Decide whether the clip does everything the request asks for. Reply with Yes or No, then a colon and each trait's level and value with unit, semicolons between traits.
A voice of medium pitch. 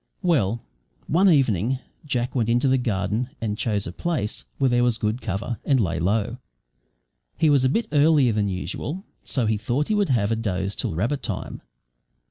No: low, 120 Hz